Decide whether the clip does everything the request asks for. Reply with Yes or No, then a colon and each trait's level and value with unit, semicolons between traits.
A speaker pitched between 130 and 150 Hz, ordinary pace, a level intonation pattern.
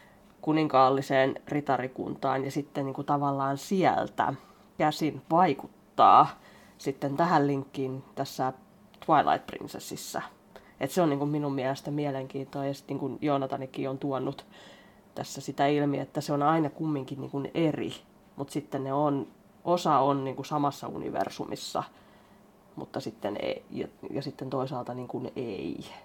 Yes: medium, 140 Hz; average, 135 wpm; narrow, 1.7 semitones